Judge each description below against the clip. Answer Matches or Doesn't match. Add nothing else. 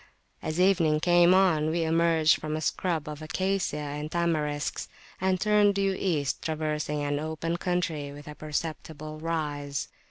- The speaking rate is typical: Matches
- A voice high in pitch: Doesn't match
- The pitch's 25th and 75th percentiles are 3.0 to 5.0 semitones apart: Doesn't match